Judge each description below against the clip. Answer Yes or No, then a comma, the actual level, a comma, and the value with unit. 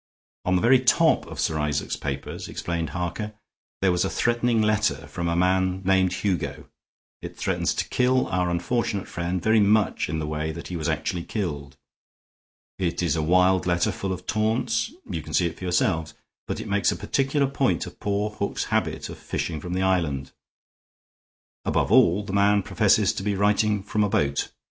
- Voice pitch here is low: Yes, very low, 95 Hz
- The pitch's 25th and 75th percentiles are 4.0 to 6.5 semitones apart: No, average, 3.6 semitones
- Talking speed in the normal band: Yes, average, 185 wpm